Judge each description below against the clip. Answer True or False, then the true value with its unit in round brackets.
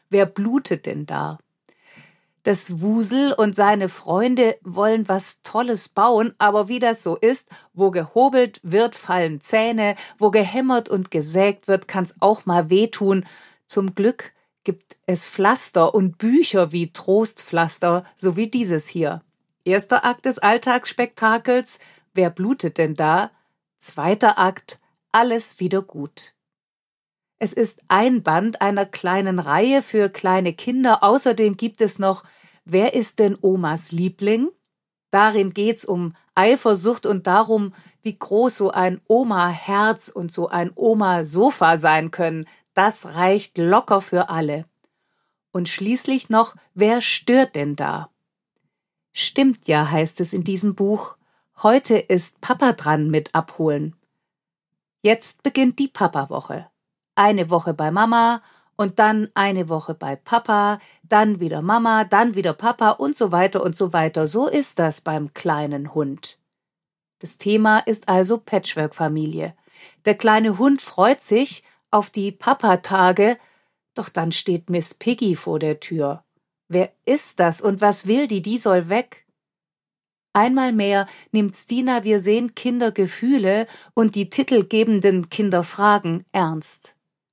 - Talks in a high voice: True (200 Hz)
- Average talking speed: True (135 wpm)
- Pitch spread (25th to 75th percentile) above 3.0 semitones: True (4.2 semitones)